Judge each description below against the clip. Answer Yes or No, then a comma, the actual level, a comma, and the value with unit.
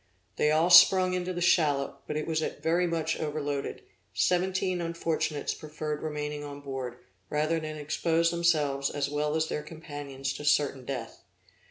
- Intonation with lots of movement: No, narrow, 2.5 semitones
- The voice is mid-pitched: Yes, medium, 155 Hz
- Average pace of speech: Yes, average, 160 wpm